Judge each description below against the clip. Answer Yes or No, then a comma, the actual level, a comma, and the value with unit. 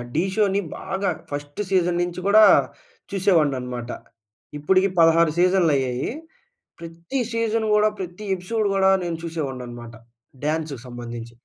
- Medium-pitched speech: Yes, medium, 170 Hz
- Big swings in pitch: Yes, wide, 5.8 semitones